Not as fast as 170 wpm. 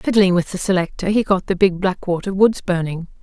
No: fast, 205 wpm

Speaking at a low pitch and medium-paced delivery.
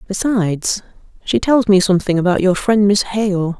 No: high, 195 Hz; average, 165 wpm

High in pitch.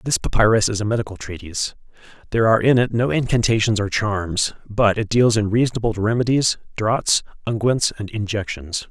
No: low, 110 Hz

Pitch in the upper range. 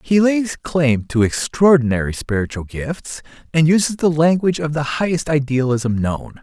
No: medium, 145 Hz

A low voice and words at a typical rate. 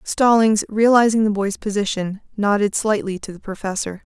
No: high, 210 Hz; average, 145 wpm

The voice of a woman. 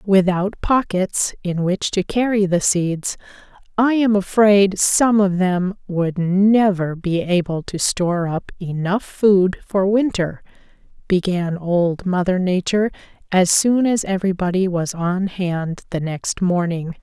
Yes: female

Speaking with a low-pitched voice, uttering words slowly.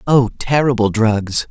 Yes: low, 120 Hz; slow, 120 wpm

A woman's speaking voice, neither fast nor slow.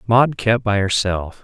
No: male; average, 170 wpm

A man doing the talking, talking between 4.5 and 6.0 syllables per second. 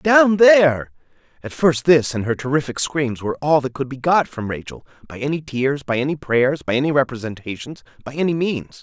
Yes: male; 5.4 syllables/s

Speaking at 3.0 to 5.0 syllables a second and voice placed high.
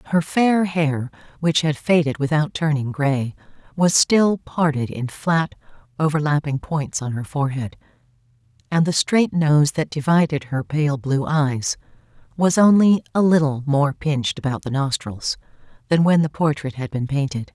No: 4.5 syllables/s; medium, 150 Hz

